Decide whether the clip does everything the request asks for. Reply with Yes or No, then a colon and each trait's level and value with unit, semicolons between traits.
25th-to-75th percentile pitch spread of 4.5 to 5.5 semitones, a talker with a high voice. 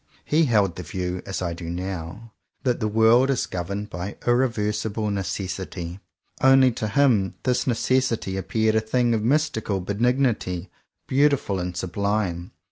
No: average, 4.8 semitones; low, 105 Hz